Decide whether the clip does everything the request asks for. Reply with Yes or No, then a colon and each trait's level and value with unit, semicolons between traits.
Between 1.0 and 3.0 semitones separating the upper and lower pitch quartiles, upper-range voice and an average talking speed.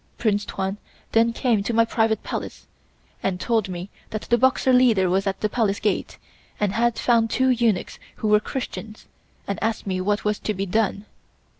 Yes: narrow, 2.6 semitones; high, 215 Hz; average, 185 wpm